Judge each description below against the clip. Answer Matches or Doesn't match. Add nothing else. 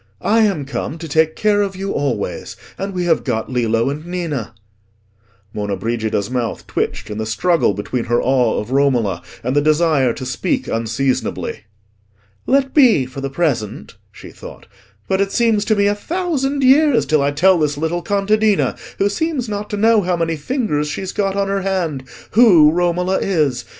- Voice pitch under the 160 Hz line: Doesn't match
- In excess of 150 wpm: Matches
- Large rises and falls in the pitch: Matches